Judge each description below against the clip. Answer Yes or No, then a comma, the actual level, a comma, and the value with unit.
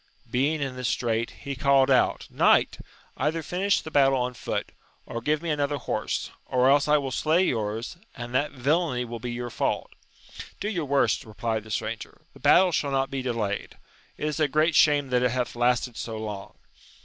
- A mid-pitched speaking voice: No, low, 130 Hz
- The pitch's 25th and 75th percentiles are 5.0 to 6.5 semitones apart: No, average, 3.9 semitones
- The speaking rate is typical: Yes, average, 195 wpm